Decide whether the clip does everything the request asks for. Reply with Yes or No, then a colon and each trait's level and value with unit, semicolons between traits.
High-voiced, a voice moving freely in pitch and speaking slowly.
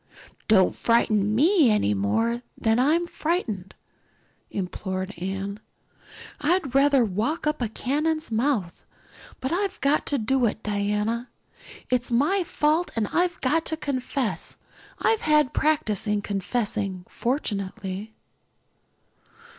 Yes: high, 235 Hz; wide, 6.6 semitones; slow, 125 wpm